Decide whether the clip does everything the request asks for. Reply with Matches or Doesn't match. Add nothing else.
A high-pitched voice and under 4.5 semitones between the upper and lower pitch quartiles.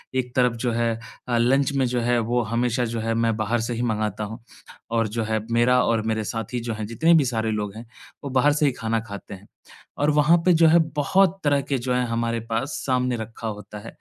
Doesn't match